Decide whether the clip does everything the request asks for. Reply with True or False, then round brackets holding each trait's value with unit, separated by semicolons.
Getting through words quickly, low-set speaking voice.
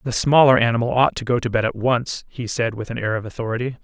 True (265 wpm; 120 Hz)